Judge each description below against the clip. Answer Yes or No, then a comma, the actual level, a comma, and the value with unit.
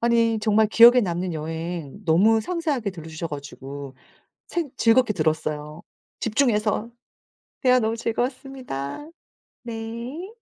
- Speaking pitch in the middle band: No, high, 220 Hz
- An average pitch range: No, wide, 6.8 semitones